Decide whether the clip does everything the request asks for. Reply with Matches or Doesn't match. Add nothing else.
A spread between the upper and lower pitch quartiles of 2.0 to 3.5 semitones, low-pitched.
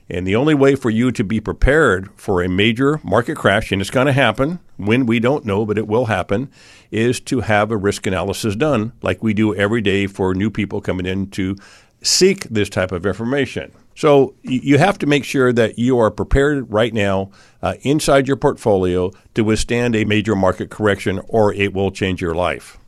Doesn't match